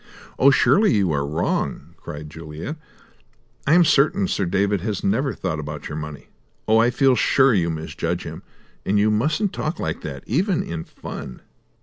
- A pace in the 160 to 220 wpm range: Yes, average, 170 wpm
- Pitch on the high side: No, low, 100 Hz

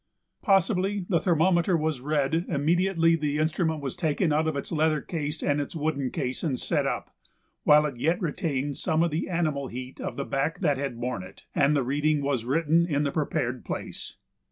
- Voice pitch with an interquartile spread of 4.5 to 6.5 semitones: No, average, 3.0 semitones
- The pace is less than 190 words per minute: No, average, 195 wpm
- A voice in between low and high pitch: Yes, medium, 150 Hz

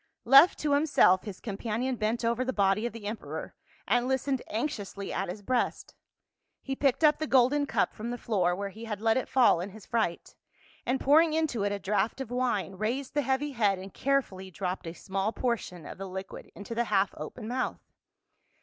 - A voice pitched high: Yes, high, 230 Hz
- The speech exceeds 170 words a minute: Yes, average, 200 wpm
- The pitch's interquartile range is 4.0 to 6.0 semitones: Yes, average, 4.8 semitones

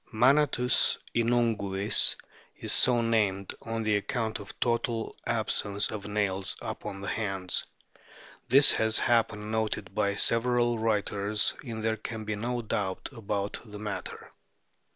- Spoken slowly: Yes, slow, 130 wpm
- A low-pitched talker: Yes, low, 110 Hz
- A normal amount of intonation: No, narrow, 2.3 semitones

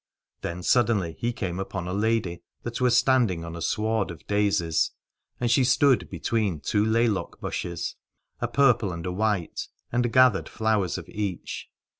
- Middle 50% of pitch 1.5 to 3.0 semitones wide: No, average, 4.8 semitones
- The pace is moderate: Yes, average, 160 wpm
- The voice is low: Yes, low, 105 Hz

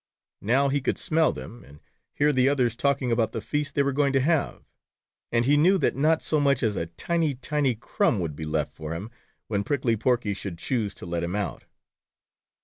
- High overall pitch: No, low, 125 Hz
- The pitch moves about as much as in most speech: No, wide, 5.8 semitones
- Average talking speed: No, fast, 210 wpm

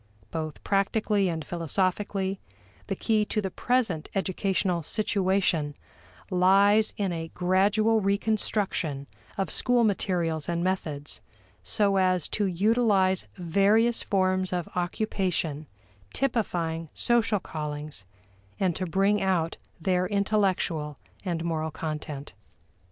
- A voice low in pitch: No, medium, 185 Hz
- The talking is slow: Yes, slow, 105 wpm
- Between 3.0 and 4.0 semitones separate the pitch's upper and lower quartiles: Yes, average, 3.7 semitones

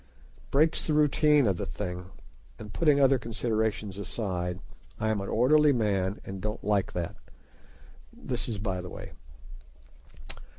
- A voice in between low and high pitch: No, low, 105 Hz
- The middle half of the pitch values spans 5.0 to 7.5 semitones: Yes, wide, 5.6 semitones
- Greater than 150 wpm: No, average, 145 wpm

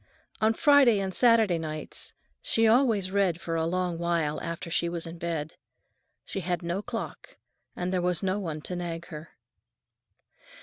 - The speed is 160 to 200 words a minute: Yes, average, 165 wpm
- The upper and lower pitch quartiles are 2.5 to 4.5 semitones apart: Yes, average, 3.2 semitones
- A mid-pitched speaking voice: Yes, medium, 175 Hz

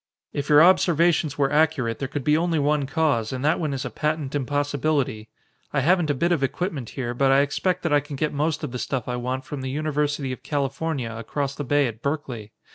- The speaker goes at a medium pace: No, fast, 225 wpm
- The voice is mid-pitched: Yes, medium, 145 Hz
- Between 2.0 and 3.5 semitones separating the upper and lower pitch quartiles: Yes, average, 2.8 semitones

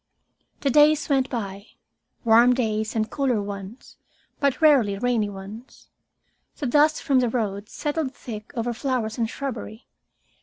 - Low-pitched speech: No, high, 240 Hz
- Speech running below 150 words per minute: Yes, average, 140 wpm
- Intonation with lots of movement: No, average, 4.0 semitones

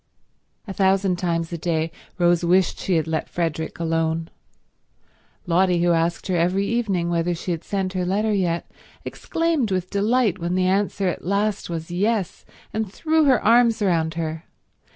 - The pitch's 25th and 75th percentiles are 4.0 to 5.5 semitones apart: No, average, 3.2 semitones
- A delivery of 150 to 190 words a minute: Yes, average, 165 wpm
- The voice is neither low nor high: Yes, medium, 180 Hz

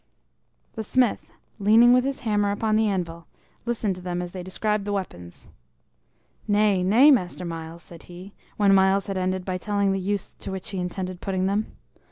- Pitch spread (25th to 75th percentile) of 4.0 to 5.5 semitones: No, narrow, 2.5 semitones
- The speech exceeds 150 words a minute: Yes, average, 185 wpm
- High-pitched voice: Yes, high, 195 Hz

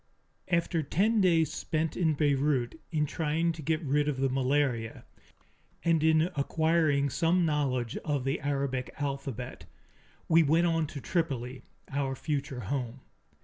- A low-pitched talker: No, medium, 145 Hz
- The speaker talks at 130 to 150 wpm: Yes, average, 140 wpm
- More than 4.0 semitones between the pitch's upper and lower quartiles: No, average, 3.2 semitones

